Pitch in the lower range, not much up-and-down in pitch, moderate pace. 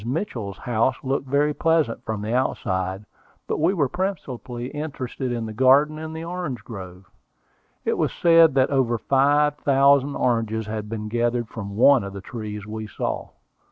No: low, 125 Hz; average, 4.8 semitones; average, 160 wpm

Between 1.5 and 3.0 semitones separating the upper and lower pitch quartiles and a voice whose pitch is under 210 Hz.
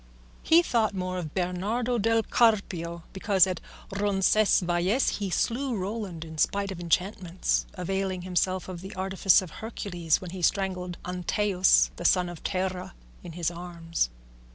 Yes: narrow, 2.4 semitones; medium, 185 Hz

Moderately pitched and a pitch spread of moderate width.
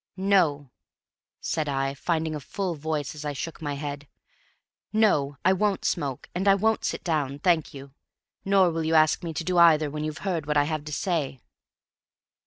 Yes: medium, 155 Hz; average, 3.6 semitones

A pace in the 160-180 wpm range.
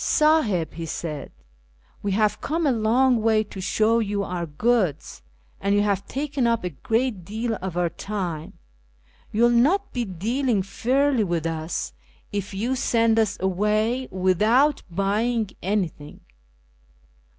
No: average, 150 wpm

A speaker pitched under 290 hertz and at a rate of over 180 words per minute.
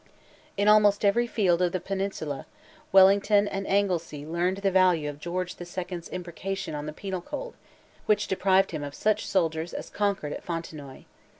No: medium, 185 Hz; average, 170 wpm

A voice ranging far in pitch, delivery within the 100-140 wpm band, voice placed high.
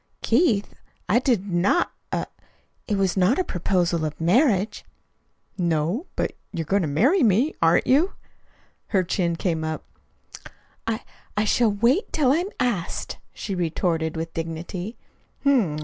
Yes: wide, 6.1 semitones; slow, 135 wpm; high, 195 Hz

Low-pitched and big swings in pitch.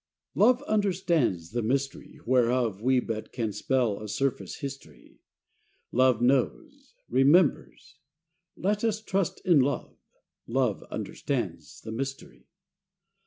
Yes: low, 130 Hz; wide, 6.6 semitones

